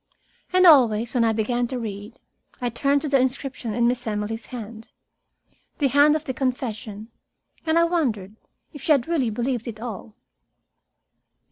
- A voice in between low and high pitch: No, high, 245 Hz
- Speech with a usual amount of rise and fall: Yes, average, 3.9 semitones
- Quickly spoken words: No, average, 160 wpm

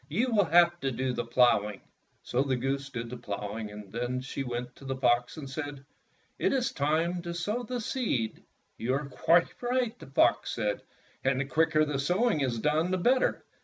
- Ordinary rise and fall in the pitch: No, wide, 5.9 semitones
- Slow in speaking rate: No, average, 200 wpm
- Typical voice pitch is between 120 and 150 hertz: Yes, medium, 140 Hz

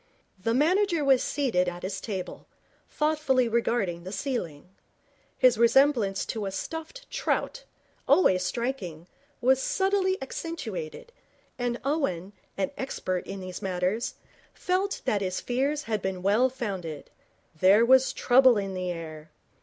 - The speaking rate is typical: No, slow, 130 wpm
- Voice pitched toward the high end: Yes, high, 235 Hz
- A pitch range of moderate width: No, wide, 6.7 semitones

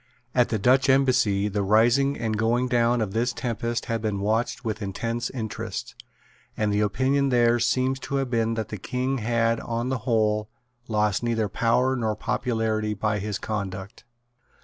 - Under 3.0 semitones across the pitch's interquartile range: Yes, narrow, 2.5 semitones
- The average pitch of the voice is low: Yes, low, 115 Hz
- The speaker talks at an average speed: Yes, average, 170 wpm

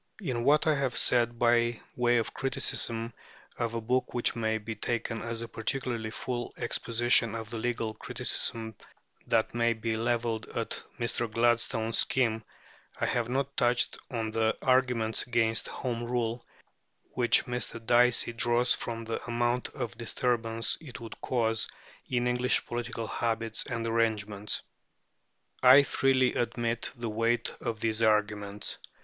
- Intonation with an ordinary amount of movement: No, narrow, 1.4 semitones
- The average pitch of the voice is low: Yes, low, 115 Hz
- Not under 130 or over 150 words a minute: Yes, average, 145 wpm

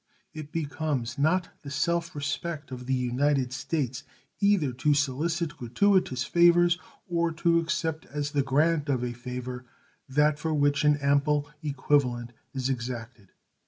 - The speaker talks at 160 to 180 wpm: No, average, 140 wpm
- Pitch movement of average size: Yes, average, 4.1 semitones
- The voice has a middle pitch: Yes, medium, 145 Hz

